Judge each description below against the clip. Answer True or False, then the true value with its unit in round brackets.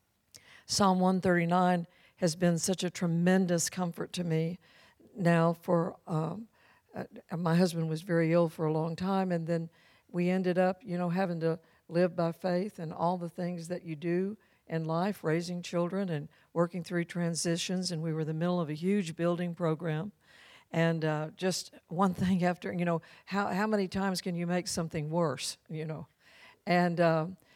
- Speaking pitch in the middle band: True (175 Hz)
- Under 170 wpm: False (180 wpm)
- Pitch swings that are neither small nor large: False (2.0 semitones)